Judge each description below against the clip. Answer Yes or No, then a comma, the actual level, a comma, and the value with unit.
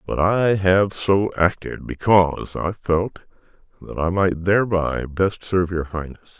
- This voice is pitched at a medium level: No, very low, 90 Hz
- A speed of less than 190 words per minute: Yes, average, 150 wpm